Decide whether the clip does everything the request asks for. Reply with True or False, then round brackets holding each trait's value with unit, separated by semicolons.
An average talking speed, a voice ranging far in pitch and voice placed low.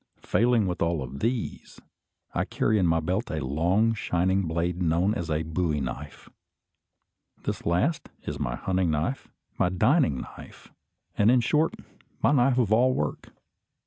True (150 wpm; 6.0 semitones; 90 Hz)